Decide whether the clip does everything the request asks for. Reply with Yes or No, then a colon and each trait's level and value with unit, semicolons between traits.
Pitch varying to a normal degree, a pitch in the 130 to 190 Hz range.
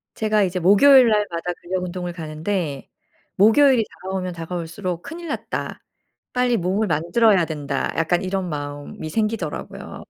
Yes: average, 4.4 semitones; medium, 185 Hz